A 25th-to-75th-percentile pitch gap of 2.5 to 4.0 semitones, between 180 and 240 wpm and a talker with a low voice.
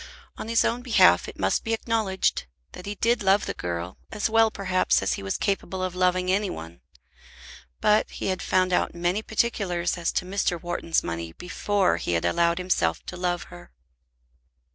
No: average, 3.3 semitones; average, 185 wpm; medium, 185 Hz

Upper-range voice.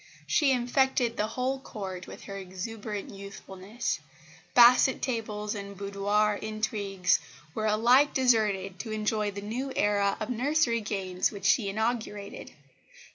Yes: high, 215 Hz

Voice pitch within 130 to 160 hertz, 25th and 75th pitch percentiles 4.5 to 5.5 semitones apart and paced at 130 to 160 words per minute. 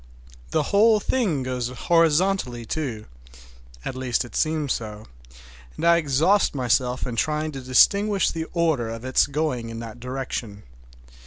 Yes: low, 135 Hz; average, 5.2 semitones; average, 145 wpm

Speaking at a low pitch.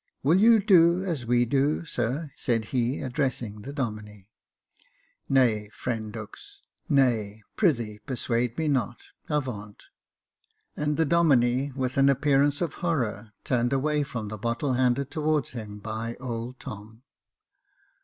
Yes: low, 125 Hz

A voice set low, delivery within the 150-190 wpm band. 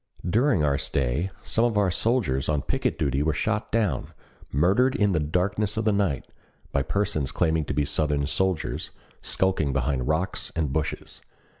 Yes: very low, 80 Hz; average, 165 wpm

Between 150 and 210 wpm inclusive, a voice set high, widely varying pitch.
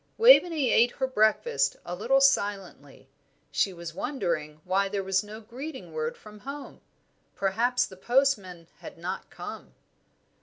No: average, 140 wpm; high, 210 Hz; wide, 6.3 semitones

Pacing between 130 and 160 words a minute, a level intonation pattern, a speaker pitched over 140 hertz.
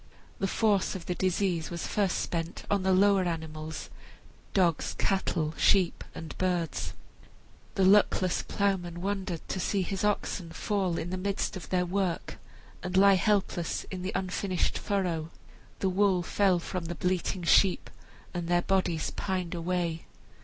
Yes: average, 150 wpm; narrow, 2.2 semitones; medium, 185 Hz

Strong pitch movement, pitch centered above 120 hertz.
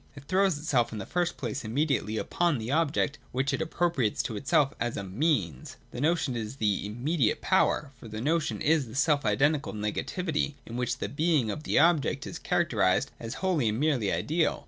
Yes: wide, 6.0 semitones; medium, 140 Hz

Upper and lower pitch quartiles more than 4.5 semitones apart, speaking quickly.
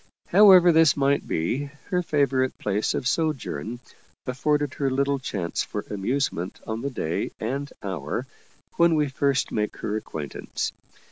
No: average, 5.3 semitones; average, 140 wpm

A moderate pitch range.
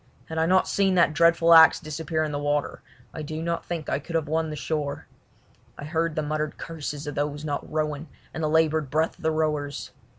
No: narrow, 1.7 semitones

